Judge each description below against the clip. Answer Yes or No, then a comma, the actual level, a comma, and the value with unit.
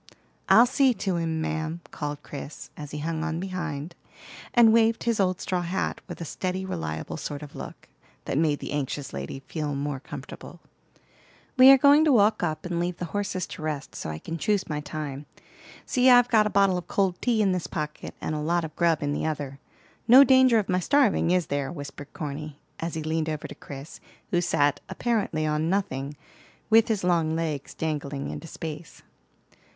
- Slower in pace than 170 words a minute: No, average, 195 wpm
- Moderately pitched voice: Yes, medium, 165 Hz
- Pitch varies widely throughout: No, average, 4.6 semitones